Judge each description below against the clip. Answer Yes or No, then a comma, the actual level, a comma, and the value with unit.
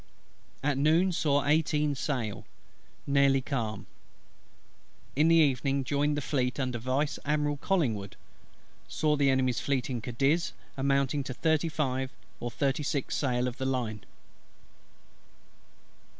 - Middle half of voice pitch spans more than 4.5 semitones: No, narrow, 2.6 semitones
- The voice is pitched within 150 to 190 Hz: No, medium, 140 Hz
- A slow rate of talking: Yes, slow, 125 wpm